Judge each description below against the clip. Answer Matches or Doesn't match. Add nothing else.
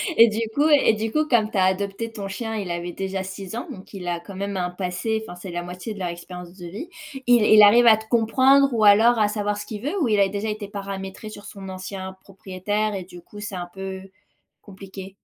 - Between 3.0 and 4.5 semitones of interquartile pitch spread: Doesn't match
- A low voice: Doesn't match